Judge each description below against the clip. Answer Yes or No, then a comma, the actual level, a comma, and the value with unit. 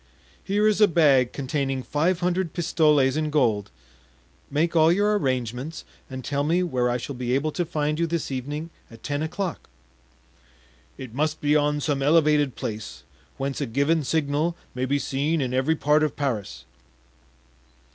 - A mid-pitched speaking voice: Yes, medium, 150 Hz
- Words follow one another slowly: No, average, 165 wpm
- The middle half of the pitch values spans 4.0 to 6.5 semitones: No, average, 3.5 semitones